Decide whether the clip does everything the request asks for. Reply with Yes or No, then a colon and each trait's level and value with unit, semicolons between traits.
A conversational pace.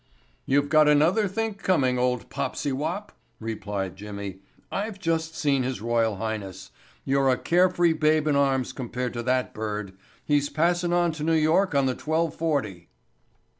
Yes: average, 165 wpm